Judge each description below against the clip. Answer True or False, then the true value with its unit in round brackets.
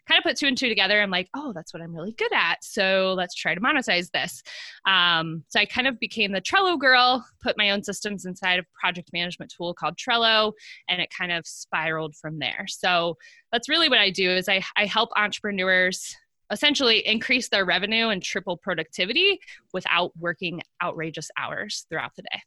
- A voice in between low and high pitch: False (200 Hz)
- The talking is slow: False (200 wpm)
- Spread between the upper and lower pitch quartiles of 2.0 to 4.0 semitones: False (5.1 semitones)